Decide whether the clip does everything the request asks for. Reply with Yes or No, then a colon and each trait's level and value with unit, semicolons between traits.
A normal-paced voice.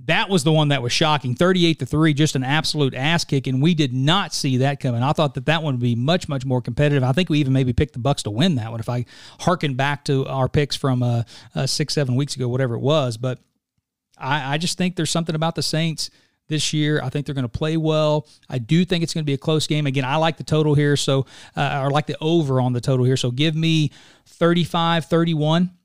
No: fast, 260 wpm